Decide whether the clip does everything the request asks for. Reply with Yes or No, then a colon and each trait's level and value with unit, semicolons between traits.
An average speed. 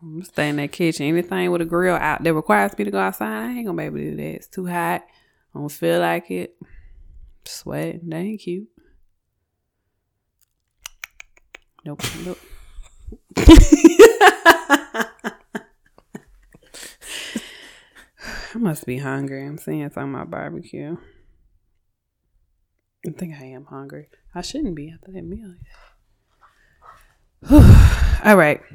No: slow, 125 wpm